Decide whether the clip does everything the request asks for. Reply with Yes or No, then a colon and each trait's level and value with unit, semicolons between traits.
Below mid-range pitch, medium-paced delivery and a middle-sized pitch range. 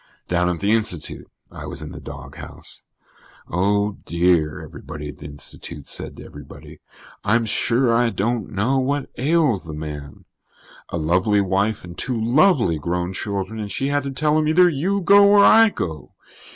No: low, 105 Hz; average, 170 wpm; wide, 7.7 semitones